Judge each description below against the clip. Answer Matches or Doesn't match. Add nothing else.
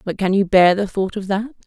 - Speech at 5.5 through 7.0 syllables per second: Matches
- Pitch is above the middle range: Matches